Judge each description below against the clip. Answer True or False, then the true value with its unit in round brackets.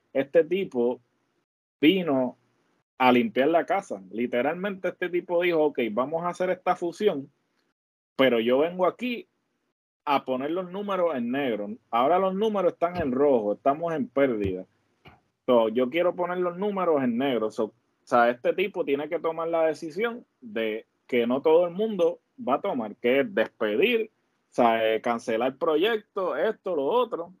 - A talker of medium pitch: True (165 Hz)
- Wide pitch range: True (6.7 semitones)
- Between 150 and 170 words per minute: True (160 wpm)